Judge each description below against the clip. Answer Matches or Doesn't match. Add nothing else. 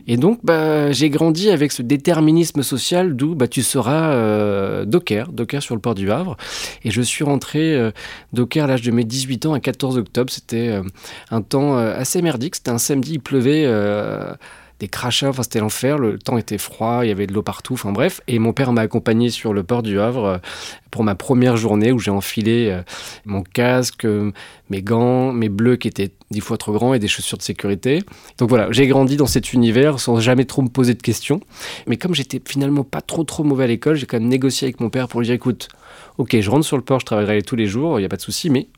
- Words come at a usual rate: Doesn't match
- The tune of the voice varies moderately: Matches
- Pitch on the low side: Matches